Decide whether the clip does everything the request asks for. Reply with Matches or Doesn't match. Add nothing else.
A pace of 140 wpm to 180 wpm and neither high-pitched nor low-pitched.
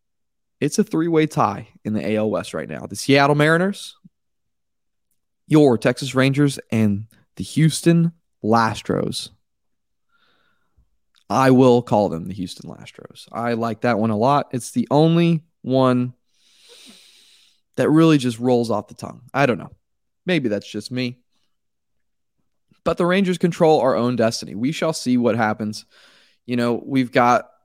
Doesn't match